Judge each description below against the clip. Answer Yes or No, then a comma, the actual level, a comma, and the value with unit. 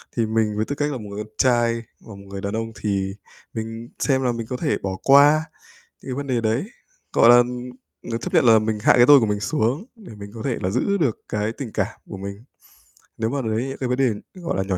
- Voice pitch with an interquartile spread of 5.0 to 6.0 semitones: No, average, 3.6 semitones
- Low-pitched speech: Yes, low, 115 Hz